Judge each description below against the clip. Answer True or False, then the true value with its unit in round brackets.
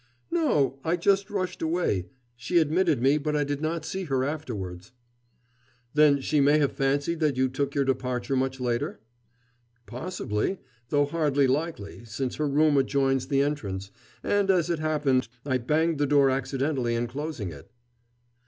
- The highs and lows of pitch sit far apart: False (3.2 semitones)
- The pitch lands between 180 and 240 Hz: False (140 Hz)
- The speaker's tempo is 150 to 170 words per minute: True (160 wpm)